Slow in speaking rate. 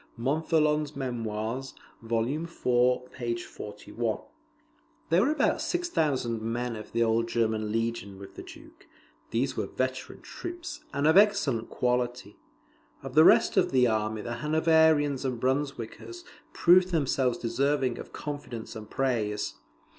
Yes: slow, 130 wpm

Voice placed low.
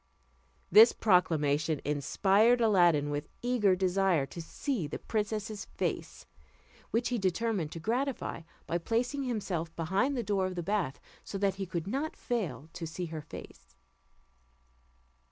No: high, 190 Hz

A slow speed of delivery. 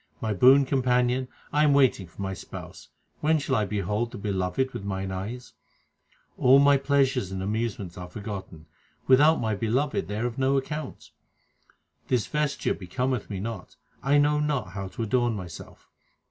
No: average, 165 wpm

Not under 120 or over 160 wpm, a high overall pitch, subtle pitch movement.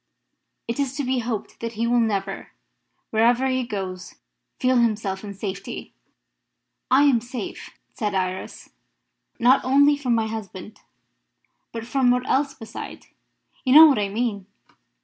No: average, 145 wpm; high, 230 Hz; average, 3.8 semitones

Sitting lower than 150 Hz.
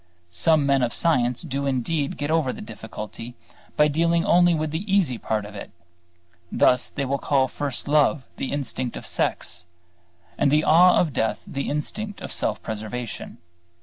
Yes: medium, 140 Hz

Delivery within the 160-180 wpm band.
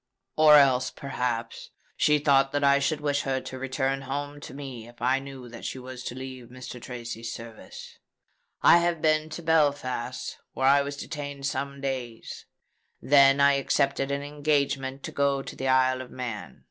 Yes: average, 175 wpm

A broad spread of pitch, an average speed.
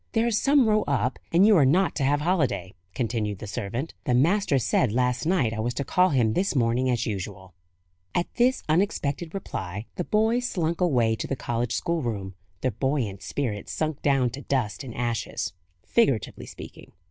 Yes: wide, 6.9 semitones; average, 180 wpm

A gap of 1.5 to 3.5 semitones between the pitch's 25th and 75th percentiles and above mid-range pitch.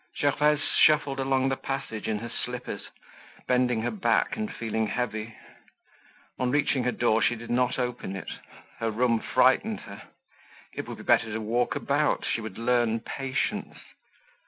No: average, 3.0 semitones; low, 125 Hz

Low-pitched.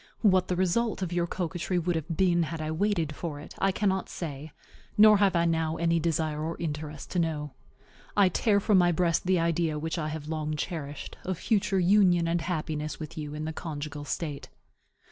No: medium, 165 Hz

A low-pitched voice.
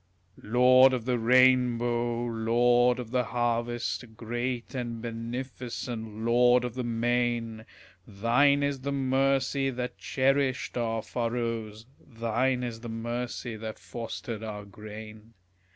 Yes: low, 120 Hz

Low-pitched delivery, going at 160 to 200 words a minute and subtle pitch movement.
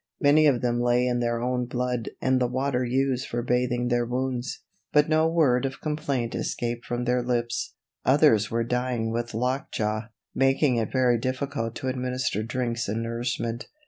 Yes: low, 125 Hz; average, 170 wpm; narrow, 1.7 semitones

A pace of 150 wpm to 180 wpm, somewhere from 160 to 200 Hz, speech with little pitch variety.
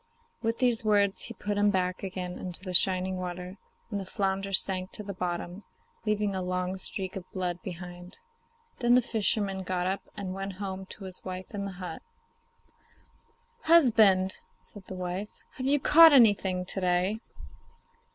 Yes: average, 165 wpm; high, 190 Hz; narrow, 2.1 semitones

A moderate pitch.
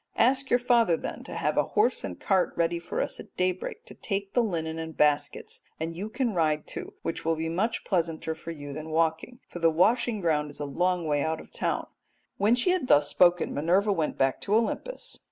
Yes: medium, 170 Hz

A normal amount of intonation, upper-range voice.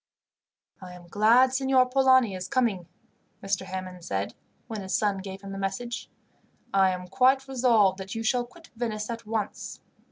Yes: average, 4.7 semitones; high, 215 Hz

